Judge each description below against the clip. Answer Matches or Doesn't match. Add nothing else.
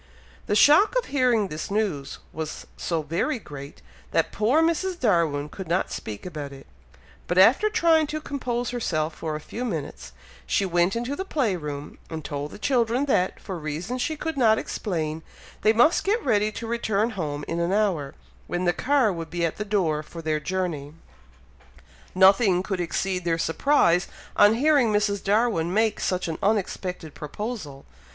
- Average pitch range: Doesn't match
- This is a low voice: Doesn't match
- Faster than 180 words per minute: Doesn't match